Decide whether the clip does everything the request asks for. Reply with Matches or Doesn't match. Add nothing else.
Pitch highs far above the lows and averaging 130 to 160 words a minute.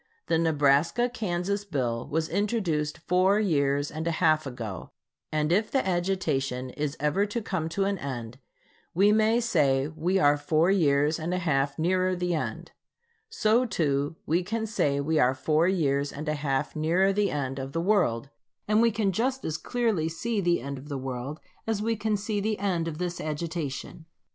Doesn't match